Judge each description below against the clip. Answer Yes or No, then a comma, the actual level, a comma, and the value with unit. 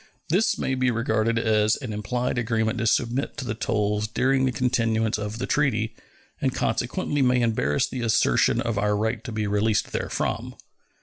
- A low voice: Yes, low, 115 Hz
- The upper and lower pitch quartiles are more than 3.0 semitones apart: No, average, 2.7 semitones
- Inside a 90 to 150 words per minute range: No, average, 175 wpm